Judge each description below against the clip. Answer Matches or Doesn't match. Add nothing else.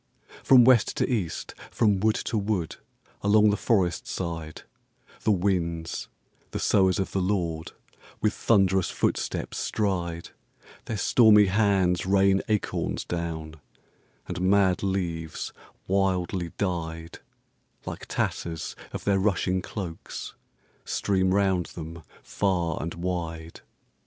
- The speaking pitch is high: Doesn't match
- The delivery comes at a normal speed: Doesn't match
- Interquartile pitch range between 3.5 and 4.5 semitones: Doesn't match